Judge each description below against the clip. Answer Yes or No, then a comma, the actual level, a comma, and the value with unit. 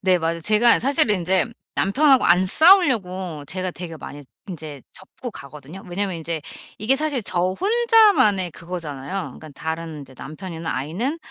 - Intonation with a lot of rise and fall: Yes, wide, 6.1 semitones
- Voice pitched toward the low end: No, medium, 185 Hz